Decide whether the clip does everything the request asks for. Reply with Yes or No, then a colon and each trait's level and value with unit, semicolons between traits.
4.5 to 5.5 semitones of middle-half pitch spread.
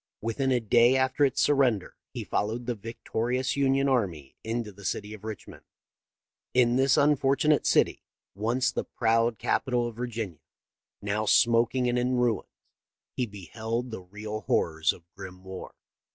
No: average, 3.3 semitones